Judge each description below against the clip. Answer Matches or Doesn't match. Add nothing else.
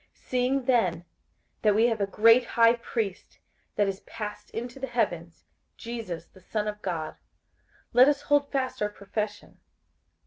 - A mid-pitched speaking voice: Doesn't match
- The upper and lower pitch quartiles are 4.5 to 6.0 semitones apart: Doesn't match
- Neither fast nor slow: Matches